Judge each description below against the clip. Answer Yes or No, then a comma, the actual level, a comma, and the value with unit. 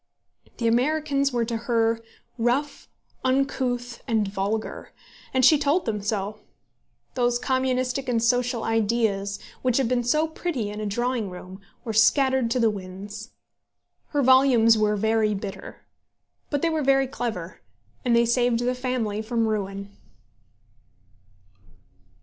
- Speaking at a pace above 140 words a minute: No, slow, 135 wpm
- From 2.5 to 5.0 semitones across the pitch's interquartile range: Yes, average, 3.3 semitones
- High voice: Yes, high, 235 Hz